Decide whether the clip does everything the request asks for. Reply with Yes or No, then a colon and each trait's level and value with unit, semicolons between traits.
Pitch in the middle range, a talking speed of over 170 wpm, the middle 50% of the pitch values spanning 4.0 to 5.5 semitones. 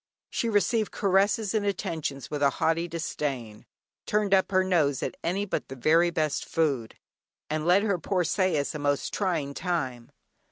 No: medium, 165 Hz; average, 165 wpm; average, 5.2 semitones